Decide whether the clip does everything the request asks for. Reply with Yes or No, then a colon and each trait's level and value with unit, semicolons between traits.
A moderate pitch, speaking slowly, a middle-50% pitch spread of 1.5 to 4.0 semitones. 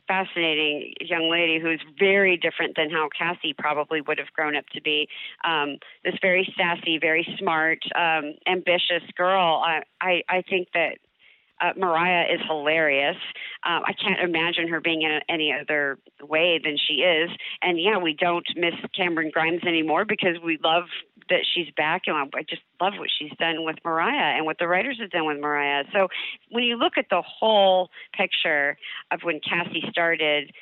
No: medium, 170 Hz; average, 180 wpm; average, 2.8 semitones